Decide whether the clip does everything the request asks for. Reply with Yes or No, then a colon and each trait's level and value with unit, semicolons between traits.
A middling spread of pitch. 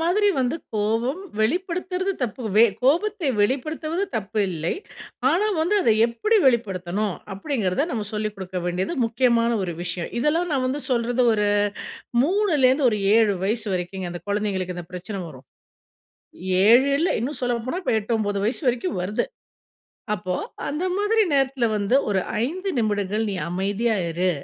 No: wide, 6.8 semitones